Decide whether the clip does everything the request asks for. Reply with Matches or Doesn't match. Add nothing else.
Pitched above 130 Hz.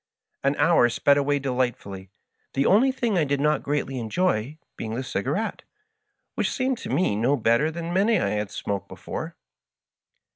Matches